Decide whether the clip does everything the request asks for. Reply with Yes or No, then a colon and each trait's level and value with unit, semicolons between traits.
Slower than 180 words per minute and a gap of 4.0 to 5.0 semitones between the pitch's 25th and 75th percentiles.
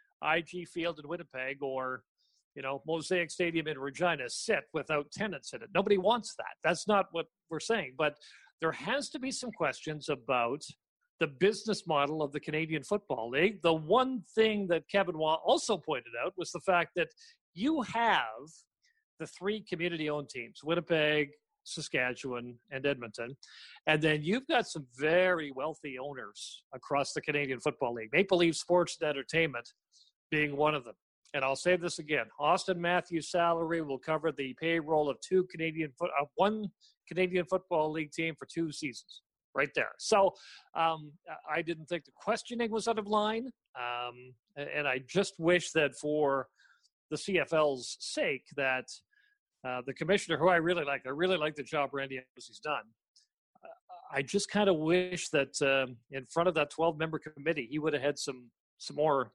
Yes: average, 170 wpm; average, 4.5 semitones